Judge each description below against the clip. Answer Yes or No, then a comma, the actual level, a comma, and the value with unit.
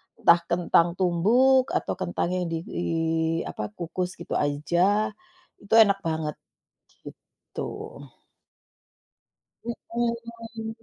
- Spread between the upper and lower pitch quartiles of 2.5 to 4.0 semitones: No, average, 5.2 semitones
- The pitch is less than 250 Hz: Yes, medium, 185 Hz